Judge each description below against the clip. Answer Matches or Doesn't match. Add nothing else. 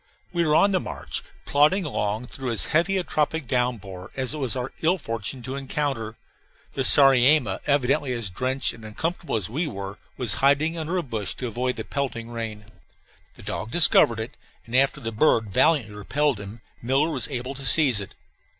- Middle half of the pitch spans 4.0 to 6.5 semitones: Matches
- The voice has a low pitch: Matches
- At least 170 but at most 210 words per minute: Matches